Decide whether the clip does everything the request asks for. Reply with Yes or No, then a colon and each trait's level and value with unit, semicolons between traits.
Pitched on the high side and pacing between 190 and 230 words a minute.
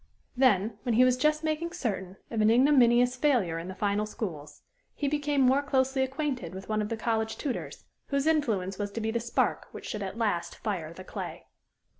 Yes: high, 230 Hz; average, 200 wpm